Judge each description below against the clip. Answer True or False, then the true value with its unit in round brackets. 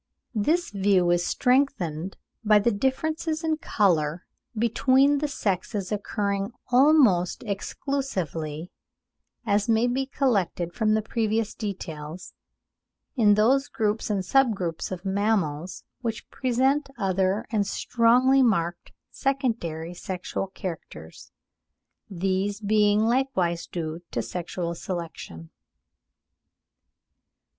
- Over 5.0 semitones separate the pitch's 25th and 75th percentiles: True (5.6 semitones)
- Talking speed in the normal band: False (100 wpm)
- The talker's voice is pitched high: True (205 Hz)